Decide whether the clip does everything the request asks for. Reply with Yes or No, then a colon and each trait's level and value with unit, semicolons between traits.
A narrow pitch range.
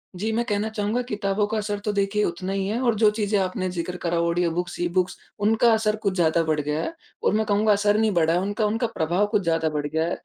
No: average, 3.7 semitones